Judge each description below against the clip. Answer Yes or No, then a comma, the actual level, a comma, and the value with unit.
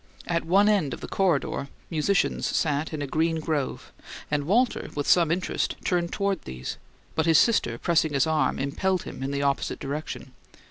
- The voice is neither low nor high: Yes, medium, 160 Hz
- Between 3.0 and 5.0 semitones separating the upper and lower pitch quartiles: Yes, average, 4.0 semitones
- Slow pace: No, average, 180 wpm